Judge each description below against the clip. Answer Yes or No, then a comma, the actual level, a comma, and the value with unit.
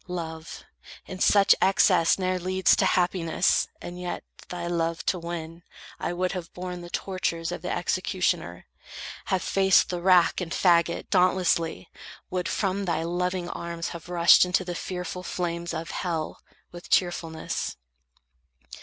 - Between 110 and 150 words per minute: Yes, average, 145 wpm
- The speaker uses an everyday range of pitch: No, narrow, 1.4 semitones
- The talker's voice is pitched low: No, medium, 175 Hz